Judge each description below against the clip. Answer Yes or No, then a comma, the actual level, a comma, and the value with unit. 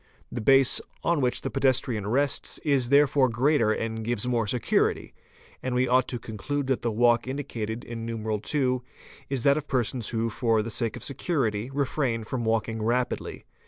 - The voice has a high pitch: No, low, 120 Hz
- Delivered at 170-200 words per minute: Yes, average, 175 wpm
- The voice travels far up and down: No, average, 3.1 semitones